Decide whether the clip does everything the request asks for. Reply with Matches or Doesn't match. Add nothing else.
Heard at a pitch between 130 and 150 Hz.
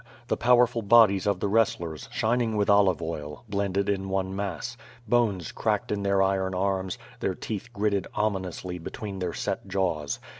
Doesn't match